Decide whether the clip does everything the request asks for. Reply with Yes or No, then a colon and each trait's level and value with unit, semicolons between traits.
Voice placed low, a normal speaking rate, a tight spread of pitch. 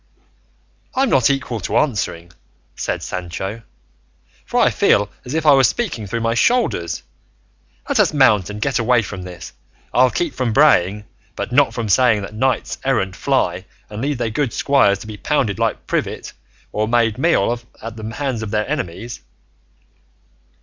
No: low, 115 Hz; average, 170 wpm; average, 4.6 semitones